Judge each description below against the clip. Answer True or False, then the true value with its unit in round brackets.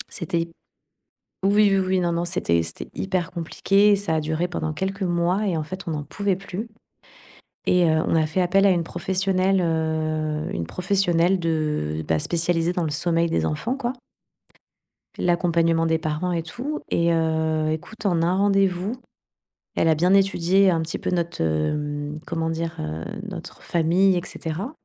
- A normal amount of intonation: True (3.0 semitones)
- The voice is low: False (170 Hz)